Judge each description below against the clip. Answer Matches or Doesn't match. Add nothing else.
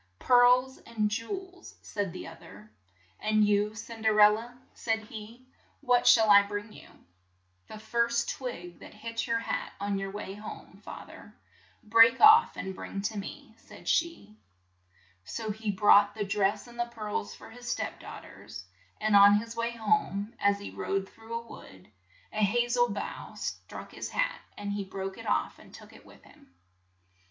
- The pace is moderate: Matches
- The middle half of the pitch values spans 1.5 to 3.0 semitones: Matches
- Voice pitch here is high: Matches